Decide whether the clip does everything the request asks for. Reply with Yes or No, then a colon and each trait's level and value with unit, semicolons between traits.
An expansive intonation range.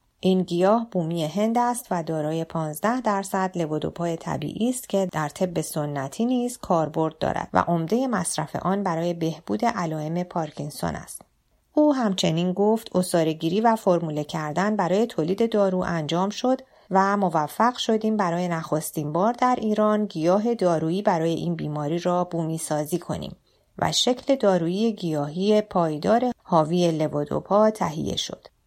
No: average, 4.7 semitones